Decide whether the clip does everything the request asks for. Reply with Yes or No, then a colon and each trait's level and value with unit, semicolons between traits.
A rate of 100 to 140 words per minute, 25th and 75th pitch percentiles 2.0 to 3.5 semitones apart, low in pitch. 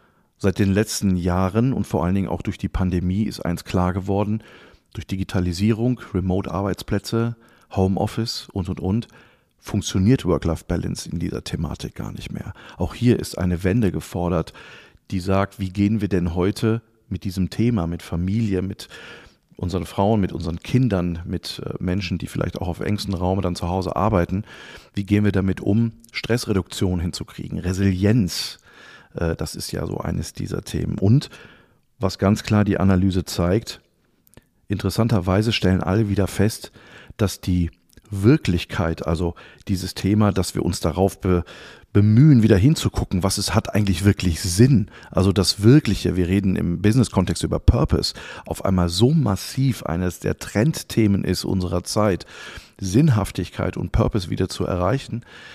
No: average, 150 wpm; average, 3.1 semitones; very low, 95 Hz